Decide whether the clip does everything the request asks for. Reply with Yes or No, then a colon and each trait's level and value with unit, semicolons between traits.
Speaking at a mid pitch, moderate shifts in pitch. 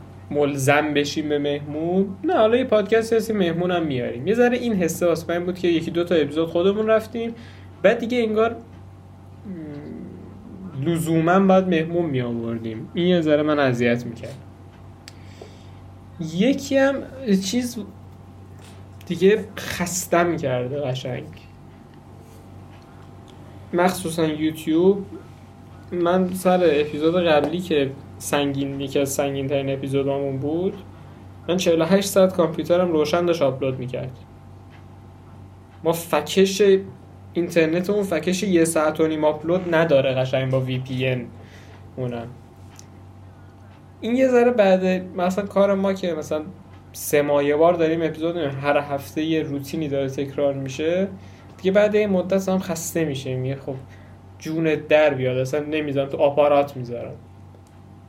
No: medium, 145 Hz; wide, 7.5 semitones